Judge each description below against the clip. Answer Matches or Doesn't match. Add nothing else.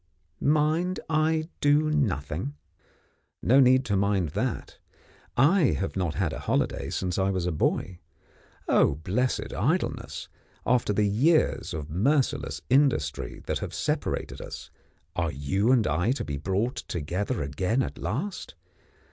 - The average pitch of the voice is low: Matches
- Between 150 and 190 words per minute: Doesn't match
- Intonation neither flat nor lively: Doesn't match